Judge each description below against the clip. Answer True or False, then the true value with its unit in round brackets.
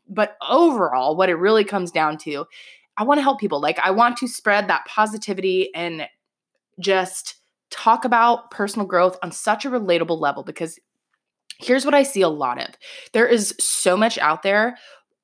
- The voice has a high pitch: True (205 Hz)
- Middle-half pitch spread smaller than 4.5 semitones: False (5.3 semitones)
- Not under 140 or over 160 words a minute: False (175 wpm)